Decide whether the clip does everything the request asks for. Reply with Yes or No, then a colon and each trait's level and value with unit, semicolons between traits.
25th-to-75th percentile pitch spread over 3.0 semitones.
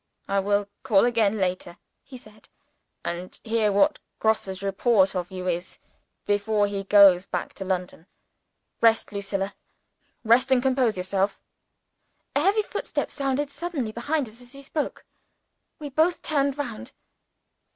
Yes: average, 5.2 semitones